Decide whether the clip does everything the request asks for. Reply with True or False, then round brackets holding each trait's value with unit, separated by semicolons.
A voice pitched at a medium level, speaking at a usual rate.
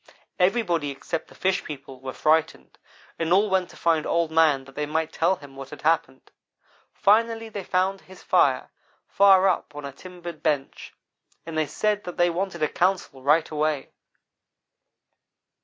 True (165 Hz; 165 wpm)